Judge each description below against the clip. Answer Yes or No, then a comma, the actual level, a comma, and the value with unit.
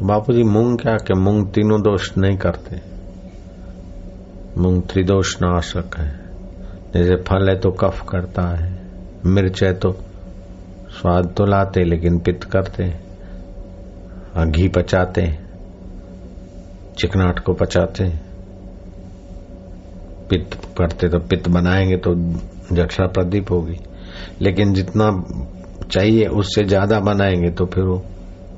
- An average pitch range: No, narrow, 0.9 semitones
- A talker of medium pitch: No, very low, 95 Hz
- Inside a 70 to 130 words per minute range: Yes, average, 115 wpm